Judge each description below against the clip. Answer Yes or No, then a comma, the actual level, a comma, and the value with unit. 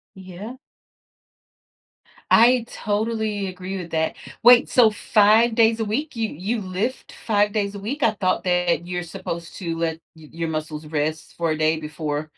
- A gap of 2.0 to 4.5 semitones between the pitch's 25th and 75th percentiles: No, average, 5.0 semitones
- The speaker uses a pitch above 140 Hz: Yes, high, 190 Hz